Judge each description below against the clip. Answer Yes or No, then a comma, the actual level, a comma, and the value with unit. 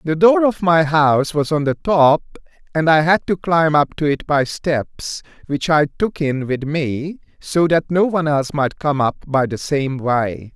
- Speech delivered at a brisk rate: Yes, fast, 210 wpm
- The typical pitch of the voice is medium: Yes, medium, 150 Hz